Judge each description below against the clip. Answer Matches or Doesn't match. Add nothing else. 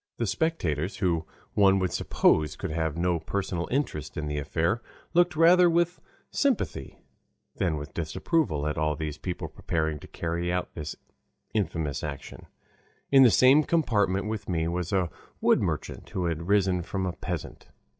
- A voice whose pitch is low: Matches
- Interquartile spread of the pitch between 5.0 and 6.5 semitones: Matches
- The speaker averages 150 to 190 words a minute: Matches